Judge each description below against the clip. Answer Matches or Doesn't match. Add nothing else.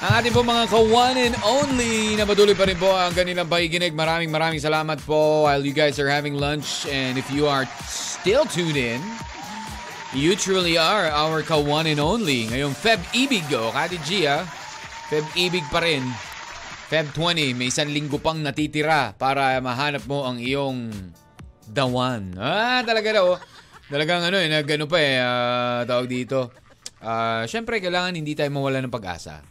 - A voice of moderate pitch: Matches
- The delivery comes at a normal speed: Doesn't match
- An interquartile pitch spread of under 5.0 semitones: Doesn't match